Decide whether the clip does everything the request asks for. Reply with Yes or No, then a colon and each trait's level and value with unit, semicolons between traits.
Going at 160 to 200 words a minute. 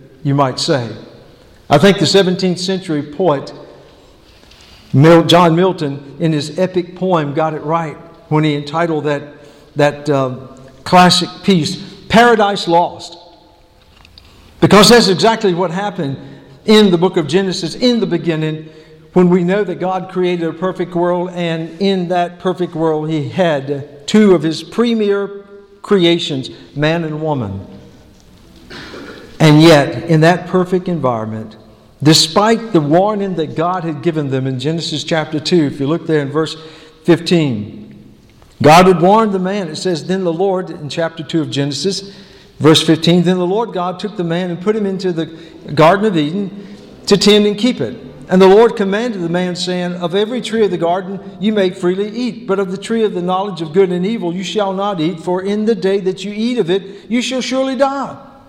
Yes: average, 175 wpm